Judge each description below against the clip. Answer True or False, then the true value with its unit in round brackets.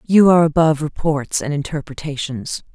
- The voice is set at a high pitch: False (150 Hz)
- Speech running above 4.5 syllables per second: True (5.5 syllables/s)